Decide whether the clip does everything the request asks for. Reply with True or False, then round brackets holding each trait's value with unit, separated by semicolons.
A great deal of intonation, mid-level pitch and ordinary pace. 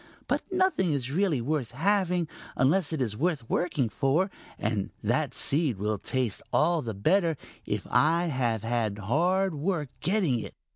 True (7.0 semitones; 150 Hz; 150 wpm)